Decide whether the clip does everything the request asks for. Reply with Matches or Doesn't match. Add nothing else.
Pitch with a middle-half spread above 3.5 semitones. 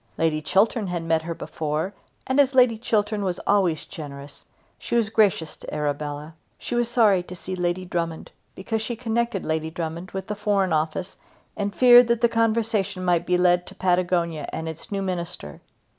Matches